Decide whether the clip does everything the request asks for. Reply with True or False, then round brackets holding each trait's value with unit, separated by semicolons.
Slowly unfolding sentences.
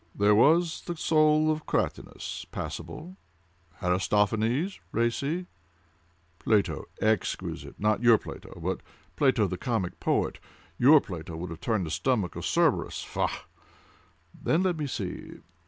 True (105 wpm)